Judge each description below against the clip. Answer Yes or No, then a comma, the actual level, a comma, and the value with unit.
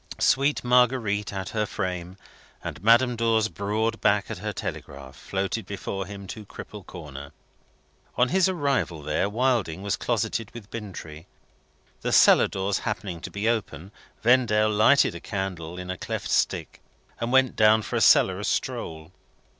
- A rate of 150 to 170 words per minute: Yes, average, 155 wpm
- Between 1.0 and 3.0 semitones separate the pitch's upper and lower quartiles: No, average, 3.9 semitones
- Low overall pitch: Yes, low, 105 Hz